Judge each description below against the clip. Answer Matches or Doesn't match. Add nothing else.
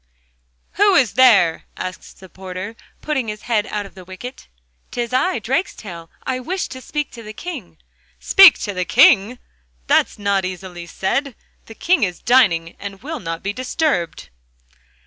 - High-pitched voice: Matches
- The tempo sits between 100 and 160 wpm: Matches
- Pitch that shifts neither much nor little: Doesn't match